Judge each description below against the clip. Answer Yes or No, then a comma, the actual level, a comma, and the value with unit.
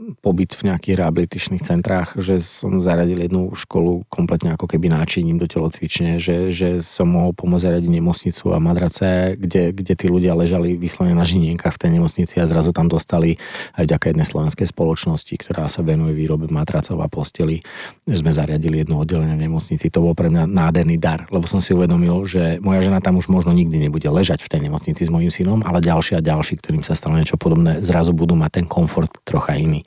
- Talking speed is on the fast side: Yes, fast, 205 wpm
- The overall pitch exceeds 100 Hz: No, very low, 85 Hz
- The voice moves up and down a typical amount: No, narrow, 1.8 semitones